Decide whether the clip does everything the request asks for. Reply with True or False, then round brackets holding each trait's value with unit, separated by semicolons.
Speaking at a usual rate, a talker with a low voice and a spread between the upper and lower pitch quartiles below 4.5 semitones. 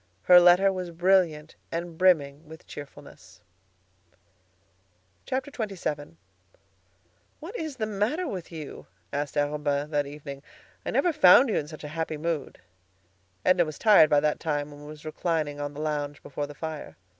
False (150 wpm; 155 Hz; 3.9 semitones)